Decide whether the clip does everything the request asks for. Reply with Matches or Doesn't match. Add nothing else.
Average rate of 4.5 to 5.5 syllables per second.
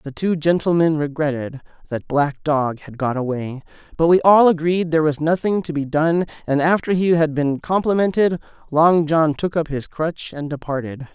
Matches